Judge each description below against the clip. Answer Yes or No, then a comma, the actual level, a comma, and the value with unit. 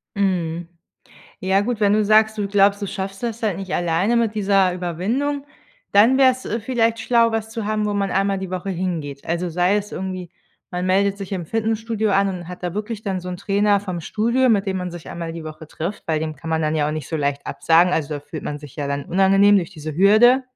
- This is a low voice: No, high, 195 Hz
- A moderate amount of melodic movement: Yes, average, 3.8 semitones